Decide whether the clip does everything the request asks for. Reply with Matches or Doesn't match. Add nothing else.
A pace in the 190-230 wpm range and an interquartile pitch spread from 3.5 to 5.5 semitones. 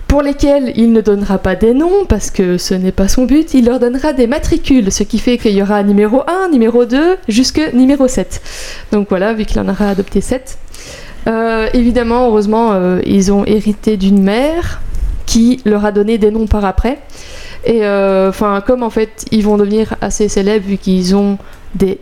Matches